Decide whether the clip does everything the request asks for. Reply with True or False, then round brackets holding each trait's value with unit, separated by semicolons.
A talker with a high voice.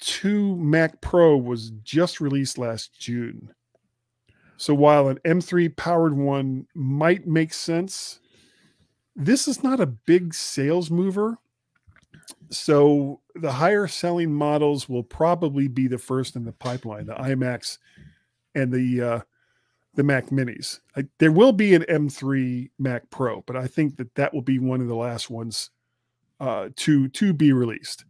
False (140 Hz)